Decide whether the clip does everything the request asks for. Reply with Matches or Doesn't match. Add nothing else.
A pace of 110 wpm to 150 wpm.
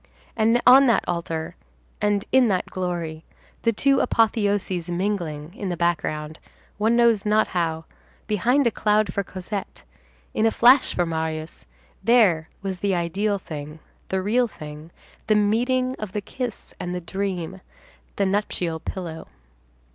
Matches